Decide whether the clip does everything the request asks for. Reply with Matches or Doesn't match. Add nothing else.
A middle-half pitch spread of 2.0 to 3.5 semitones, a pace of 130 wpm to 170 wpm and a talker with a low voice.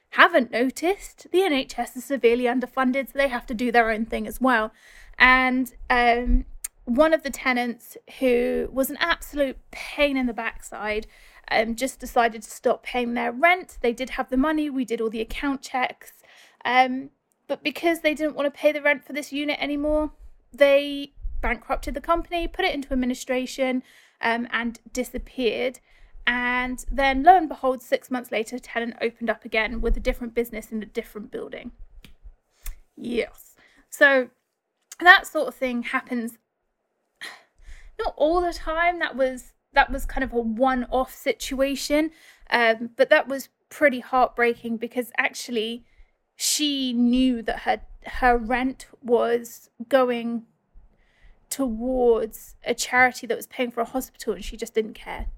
Doesn't match